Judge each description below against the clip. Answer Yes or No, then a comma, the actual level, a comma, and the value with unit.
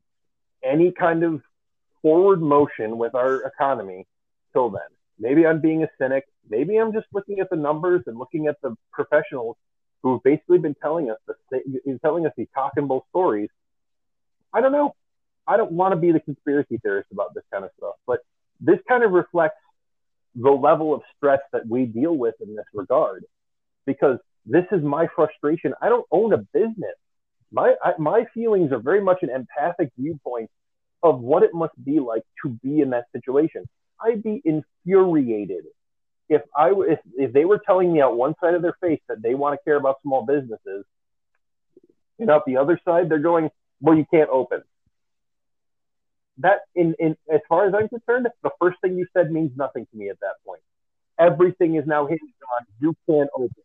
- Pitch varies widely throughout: Yes, wide, 5.8 semitones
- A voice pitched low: No, medium, 160 Hz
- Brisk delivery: No, average, 185 wpm